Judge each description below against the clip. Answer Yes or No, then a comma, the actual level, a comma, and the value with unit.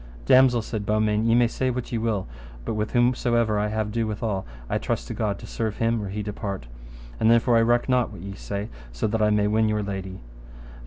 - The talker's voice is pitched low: Yes, low, 110 Hz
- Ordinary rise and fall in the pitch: No, narrow, 2.1 semitones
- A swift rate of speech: Yes, fast, 225 wpm